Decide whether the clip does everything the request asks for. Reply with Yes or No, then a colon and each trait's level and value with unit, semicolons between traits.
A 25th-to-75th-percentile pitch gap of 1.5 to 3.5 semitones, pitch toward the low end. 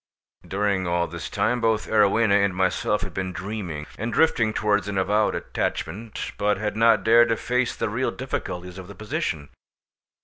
Yes: average, 3.1 semitones; low, 105 Hz